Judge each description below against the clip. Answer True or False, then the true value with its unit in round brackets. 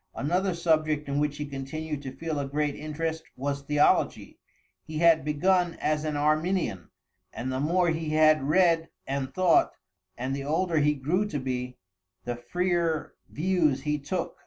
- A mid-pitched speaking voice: True (150 Hz)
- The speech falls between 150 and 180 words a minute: True (160 wpm)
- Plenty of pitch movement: False (2.9 semitones)